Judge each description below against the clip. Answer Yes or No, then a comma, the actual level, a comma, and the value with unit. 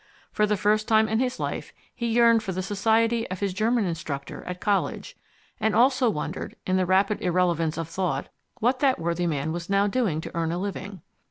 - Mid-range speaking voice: No, high, 200 Hz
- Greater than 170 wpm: Yes, average, 200 wpm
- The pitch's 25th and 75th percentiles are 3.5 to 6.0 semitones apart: Yes, average, 4.3 semitones